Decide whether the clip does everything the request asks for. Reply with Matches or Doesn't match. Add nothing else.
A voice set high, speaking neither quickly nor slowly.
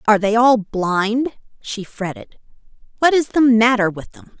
Matches